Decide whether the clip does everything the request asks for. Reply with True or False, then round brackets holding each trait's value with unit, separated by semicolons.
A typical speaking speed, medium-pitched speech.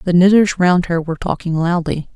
True (195 wpm; 175 Hz)